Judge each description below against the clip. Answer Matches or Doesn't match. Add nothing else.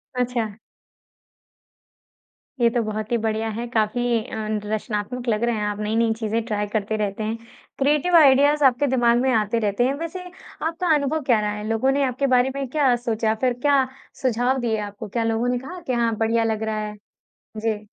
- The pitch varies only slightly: Doesn't match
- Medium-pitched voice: Doesn't match